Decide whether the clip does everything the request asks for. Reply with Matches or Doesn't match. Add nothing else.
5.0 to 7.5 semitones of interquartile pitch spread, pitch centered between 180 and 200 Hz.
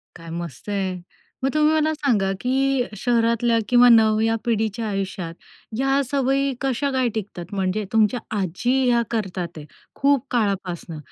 Doesn't match